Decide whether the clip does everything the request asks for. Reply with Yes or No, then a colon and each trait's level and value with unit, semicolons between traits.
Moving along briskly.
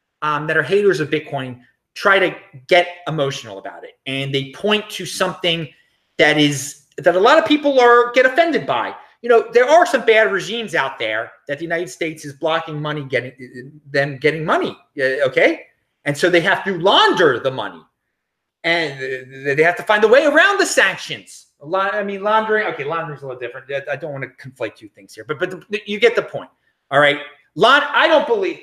Yes: fast, 210 wpm